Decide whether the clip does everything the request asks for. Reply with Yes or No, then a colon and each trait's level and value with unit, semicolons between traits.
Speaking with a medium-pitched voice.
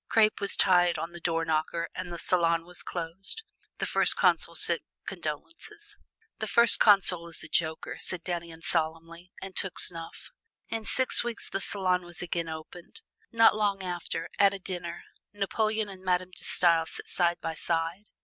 Yes: medium, 180 Hz